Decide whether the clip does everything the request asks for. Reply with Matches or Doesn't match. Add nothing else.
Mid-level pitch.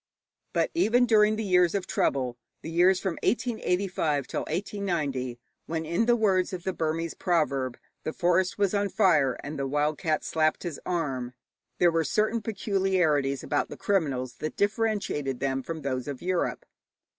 Matches